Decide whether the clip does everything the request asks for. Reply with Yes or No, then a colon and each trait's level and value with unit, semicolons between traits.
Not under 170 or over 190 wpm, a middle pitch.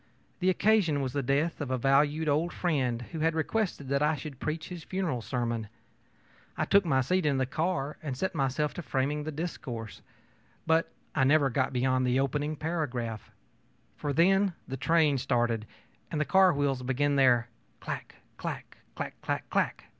Yes: average, 175 wpm; medium, 145 Hz